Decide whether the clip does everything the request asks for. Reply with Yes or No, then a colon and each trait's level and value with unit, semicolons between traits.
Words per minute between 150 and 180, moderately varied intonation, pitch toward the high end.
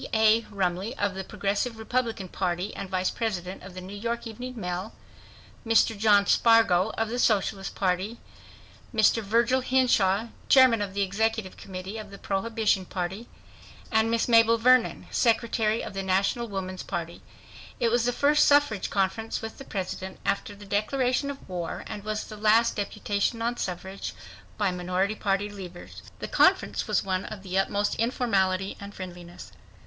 Yes: average, 160 wpm; average, 3.1 semitones; high, 205 Hz